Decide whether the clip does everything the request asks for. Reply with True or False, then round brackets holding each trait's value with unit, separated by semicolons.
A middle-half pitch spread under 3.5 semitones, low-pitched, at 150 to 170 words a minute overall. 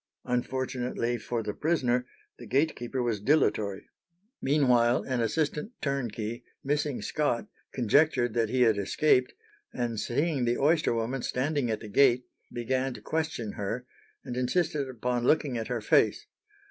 False (3.0 semitones; 125 Hz; 140 wpm)